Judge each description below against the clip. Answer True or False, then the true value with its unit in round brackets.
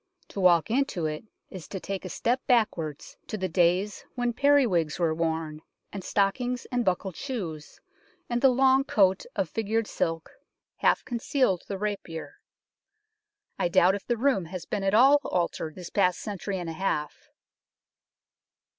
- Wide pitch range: True (5.7 semitones)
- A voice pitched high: True (195 Hz)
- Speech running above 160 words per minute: False (155 wpm)